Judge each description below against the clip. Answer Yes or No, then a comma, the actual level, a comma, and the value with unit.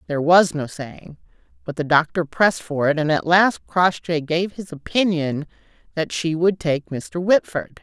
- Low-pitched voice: No, medium, 165 Hz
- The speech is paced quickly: No, average, 175 wpm